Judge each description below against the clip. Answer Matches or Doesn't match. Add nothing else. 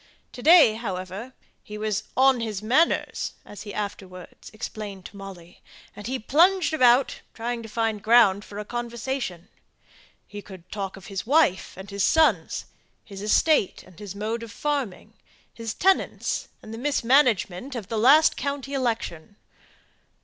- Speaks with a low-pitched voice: Doesn't match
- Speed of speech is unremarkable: Matches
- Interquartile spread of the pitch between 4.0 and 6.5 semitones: Matches